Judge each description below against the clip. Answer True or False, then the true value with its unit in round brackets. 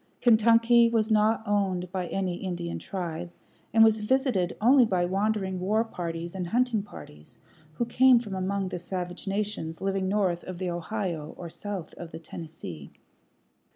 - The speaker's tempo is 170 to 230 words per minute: False (155 wpm)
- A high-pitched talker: True (195 Hz)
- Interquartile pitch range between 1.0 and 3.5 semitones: False (3.9 semitones)